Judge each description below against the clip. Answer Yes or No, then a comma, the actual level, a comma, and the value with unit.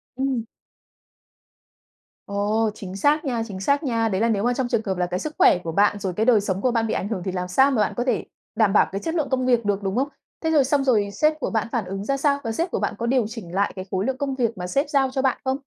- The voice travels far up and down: No, average, 4.9 semitones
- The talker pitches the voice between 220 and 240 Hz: Yes, high, 230 Hz